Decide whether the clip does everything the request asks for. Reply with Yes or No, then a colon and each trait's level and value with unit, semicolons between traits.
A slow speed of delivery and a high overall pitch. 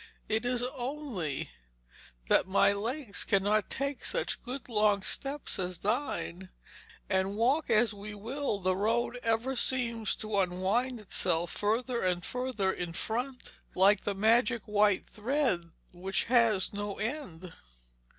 Yes: slow, 130 wpm; high, 215 Hz